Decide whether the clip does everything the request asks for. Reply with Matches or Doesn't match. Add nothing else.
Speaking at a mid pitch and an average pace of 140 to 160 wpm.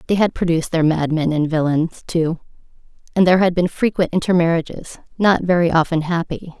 Matches